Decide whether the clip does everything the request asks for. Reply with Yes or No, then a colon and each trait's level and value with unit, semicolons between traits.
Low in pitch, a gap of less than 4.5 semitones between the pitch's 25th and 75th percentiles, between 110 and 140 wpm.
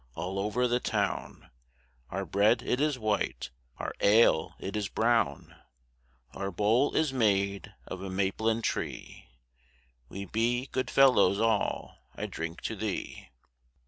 Yes: low, 105 Hz; average, 3.7 semitones; slow, 135 wpm